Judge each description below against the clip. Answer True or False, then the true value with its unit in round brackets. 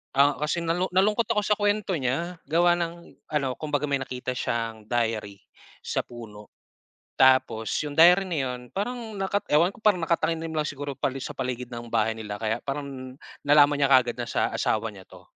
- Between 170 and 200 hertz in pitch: False (140 Hz)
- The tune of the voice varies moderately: False (6.2 semitones)